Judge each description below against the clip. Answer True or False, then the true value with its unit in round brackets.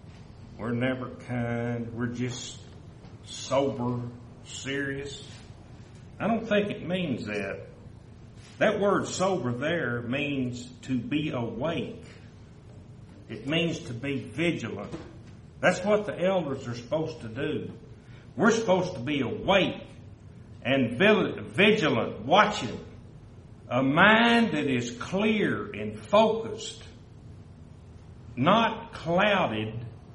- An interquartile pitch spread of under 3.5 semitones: False (5.5 semitones)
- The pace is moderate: False (100 wpm)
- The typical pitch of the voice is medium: False (125 Hz)